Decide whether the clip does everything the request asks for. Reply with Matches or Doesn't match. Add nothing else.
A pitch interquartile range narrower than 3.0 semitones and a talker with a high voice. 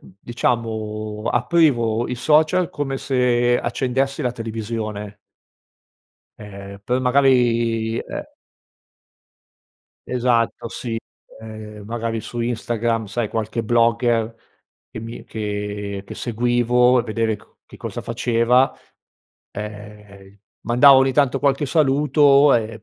Doesn't match